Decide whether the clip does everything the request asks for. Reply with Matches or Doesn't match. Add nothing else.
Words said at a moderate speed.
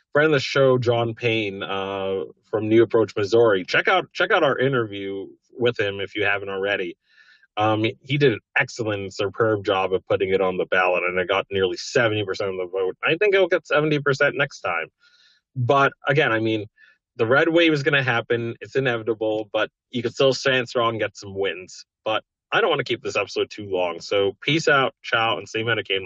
Doesn't match